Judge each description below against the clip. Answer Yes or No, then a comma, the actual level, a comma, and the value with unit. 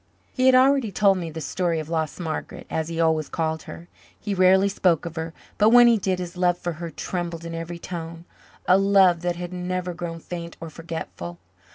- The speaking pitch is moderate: Yes, medium, 175 Hz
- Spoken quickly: Yes, fast, 210 wpm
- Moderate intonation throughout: No, narrow, 2.1 semitones